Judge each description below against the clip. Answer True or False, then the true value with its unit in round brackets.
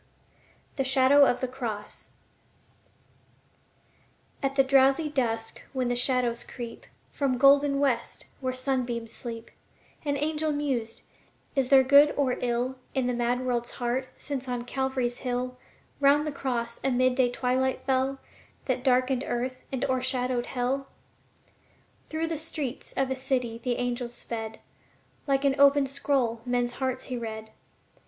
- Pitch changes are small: True (1.9 semitones)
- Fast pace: False (145 wpm)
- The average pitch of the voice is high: True (255 Hz)